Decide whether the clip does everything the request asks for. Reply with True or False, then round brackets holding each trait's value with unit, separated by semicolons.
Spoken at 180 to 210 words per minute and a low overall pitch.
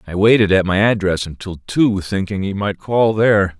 True (200 wpm; 100 Hz)